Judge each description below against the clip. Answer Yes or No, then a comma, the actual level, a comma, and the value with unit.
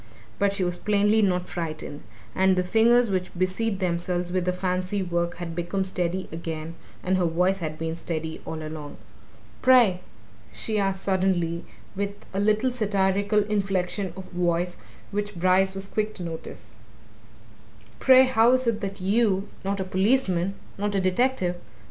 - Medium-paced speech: Yes, average, 160 wpm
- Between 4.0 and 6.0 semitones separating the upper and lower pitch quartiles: No, narrow, 2.6 semitones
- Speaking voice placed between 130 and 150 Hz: No, high, 190 Hz